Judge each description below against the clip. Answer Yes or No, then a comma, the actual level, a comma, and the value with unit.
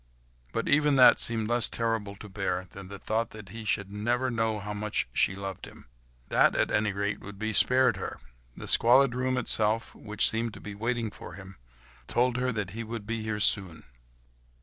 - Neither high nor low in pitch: No, low, 110 Hz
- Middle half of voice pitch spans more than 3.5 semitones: No, average, 2.7 semitones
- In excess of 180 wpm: Yes, average, 195 wpm